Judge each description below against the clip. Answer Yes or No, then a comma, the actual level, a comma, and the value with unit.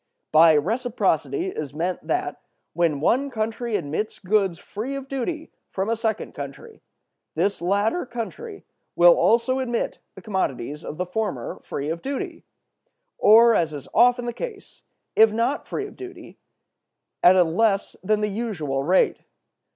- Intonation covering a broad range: Yes, wide, 6.1 semitones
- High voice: Yes, high, 215 Hz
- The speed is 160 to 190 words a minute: No, average, 150 wpm